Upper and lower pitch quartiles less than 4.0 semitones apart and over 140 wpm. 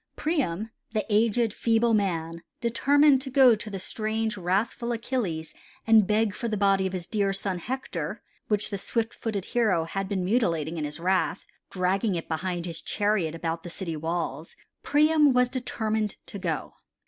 No: average, 4.6 semitones; average, 170 wpm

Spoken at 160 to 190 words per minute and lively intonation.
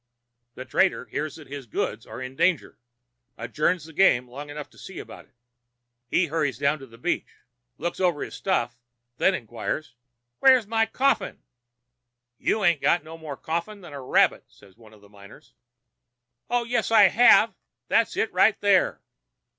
Yes: average, 170 wpm; wide, 6.9 semitones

